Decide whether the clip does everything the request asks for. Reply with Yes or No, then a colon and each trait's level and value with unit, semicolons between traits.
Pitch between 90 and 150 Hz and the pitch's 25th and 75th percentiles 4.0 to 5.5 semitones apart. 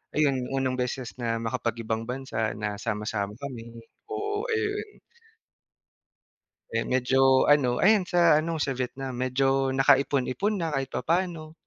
Yes: low, 135 Hz; average, 4.3 semitones